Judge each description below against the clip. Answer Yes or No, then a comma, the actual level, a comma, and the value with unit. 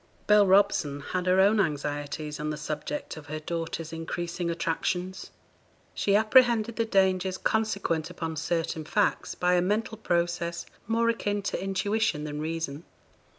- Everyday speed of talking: Yes, average, 145 wpm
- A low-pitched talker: No, medium, 175 Hz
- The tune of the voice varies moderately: Yes, average, 4.4 semitones